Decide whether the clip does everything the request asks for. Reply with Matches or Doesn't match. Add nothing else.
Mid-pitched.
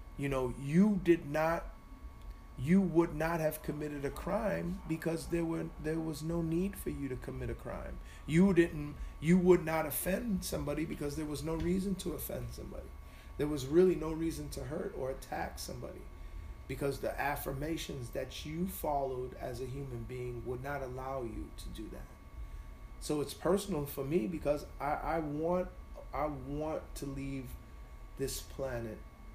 Matches